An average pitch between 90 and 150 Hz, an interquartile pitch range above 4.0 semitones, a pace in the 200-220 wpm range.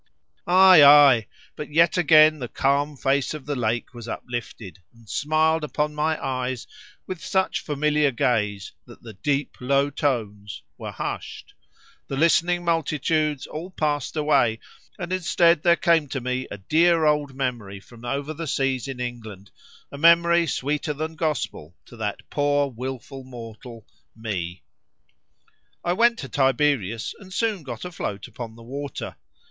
No: medium, 140 Hz; average, 4.6 semitones; average, 150 wpm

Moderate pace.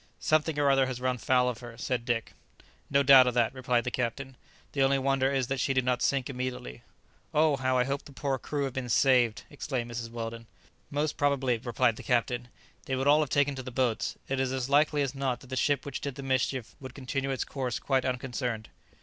No: fast, 225 wpm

